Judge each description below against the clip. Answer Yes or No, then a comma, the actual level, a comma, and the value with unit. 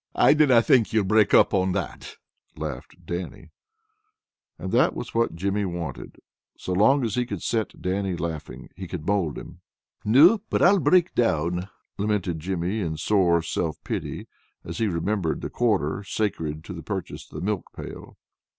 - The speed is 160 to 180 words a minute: Yes, average, 170 wpm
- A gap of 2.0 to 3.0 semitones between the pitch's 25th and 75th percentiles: No, average, 4.5 semitones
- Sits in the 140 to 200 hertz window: No, very low, 95 Hz